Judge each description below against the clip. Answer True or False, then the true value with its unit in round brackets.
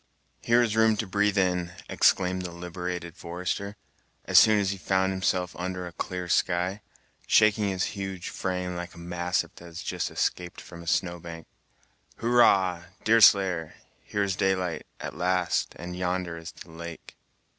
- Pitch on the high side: False (90 Hz)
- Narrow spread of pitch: True (1.8 semitones)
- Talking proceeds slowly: False (155 wpm)